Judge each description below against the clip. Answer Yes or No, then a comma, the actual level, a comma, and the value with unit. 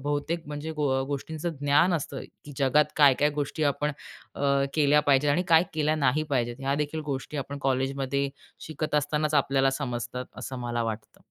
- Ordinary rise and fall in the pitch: No, narrow, 2.0 semitones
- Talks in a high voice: No, medium, 145 Hz